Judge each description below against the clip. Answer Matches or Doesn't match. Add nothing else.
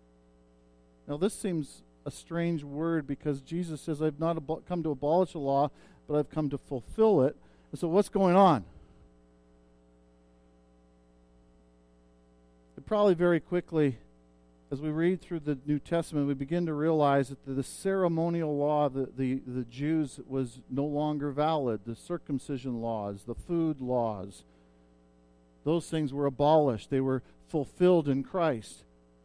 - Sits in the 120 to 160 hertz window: Matches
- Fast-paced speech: Doesn't match